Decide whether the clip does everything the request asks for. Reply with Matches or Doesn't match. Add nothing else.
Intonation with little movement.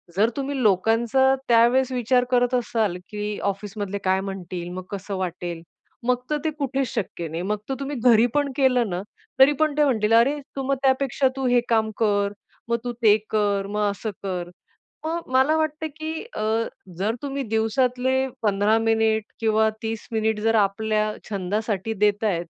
Doesn't match